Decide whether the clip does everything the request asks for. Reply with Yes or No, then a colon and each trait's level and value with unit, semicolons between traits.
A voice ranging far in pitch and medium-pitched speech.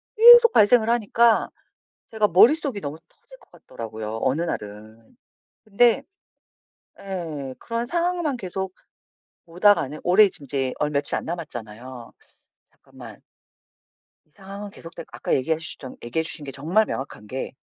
Yes: wide, 8.6 semitones; medium, 170 Hz